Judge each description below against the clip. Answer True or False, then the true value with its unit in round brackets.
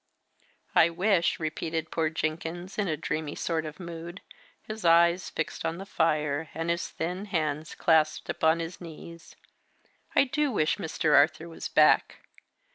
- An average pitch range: False (1.7 semitones)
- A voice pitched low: False (165 Hz)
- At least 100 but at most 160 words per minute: True (150 wpm)